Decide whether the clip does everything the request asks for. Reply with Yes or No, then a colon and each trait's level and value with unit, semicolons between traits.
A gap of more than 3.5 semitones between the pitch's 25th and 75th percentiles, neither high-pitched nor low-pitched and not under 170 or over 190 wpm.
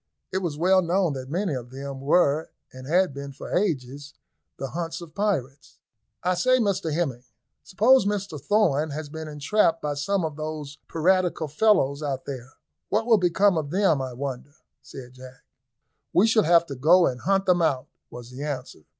Yes: average, 5.1 semitones; medium, 155 Hz; average, 175 wpm